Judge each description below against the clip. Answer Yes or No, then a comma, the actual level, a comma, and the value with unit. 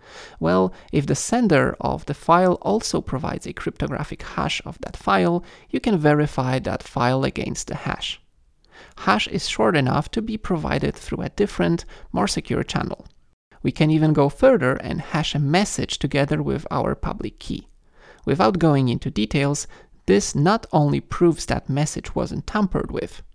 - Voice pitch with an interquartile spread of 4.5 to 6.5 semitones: Yes, wide, 5.6 semitones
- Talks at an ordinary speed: Yes, average, 160 wpm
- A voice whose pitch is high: No, medium, 145 Hz